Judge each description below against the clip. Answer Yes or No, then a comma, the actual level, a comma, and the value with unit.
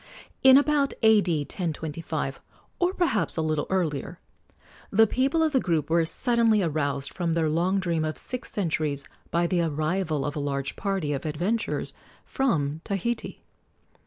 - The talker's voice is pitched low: No, medium, 170 Hz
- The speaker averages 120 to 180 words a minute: Yes, average, 150 wpm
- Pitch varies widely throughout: Yes, wide, 6.2 semitones